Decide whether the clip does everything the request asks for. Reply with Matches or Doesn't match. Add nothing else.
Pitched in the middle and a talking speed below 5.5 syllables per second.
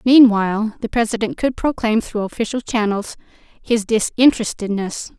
Doesn't match